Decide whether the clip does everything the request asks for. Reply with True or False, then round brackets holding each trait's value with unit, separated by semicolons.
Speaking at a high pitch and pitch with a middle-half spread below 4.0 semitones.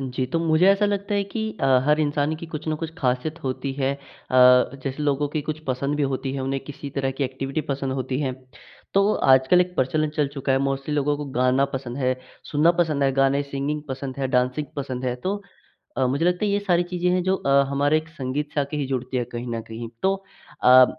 False (140 Hz; 3.0 semitones)